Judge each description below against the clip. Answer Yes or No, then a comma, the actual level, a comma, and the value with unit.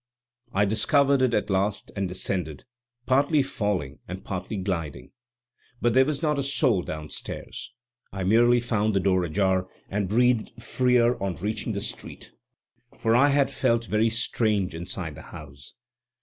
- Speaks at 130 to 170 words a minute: Yes, average, 150 wpm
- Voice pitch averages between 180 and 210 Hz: No, low, 105 Hz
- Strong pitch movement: No, average, 4.8 semitones